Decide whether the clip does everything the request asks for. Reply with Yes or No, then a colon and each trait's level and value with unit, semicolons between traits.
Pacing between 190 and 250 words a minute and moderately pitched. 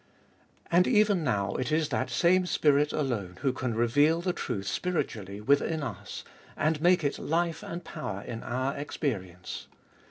No: average, 155 wpm; medium, 145 Hz